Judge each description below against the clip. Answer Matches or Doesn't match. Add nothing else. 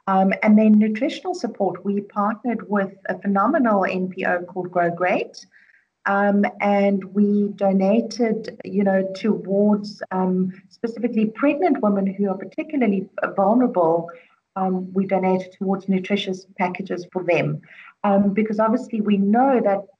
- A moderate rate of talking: Doesn't match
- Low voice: Doesn't match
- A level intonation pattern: Matches